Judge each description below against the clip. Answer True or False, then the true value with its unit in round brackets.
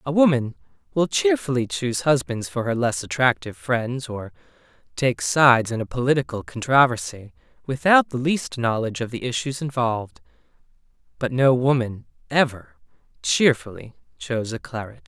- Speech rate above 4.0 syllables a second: True (5.2 syllables/s)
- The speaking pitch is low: True (125 Hz)